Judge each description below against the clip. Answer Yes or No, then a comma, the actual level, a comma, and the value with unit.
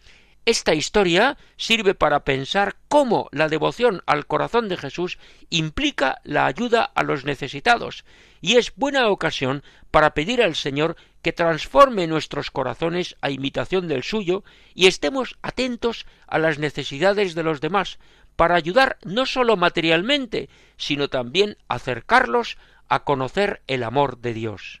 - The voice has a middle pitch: Yes, medium, 175 Hz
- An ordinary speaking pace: Yes, average, 140 wpm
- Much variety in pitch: Yes, wide, 7.7 semitones